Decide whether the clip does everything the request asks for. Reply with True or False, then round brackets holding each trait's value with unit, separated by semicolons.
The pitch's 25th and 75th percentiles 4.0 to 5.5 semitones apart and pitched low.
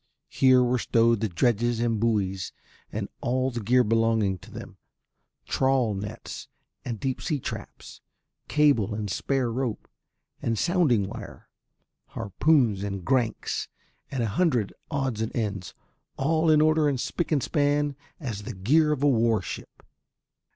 True (4.5 semitones; 120 Hz)